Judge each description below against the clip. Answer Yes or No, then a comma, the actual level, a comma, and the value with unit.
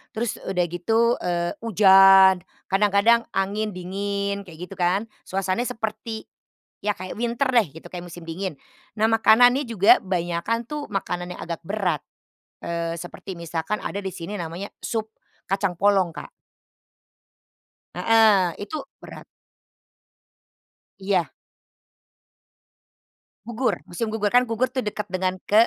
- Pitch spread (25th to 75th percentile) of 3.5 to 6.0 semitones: Yes, average, 3.9 semitones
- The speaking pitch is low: No, high, 195 Hz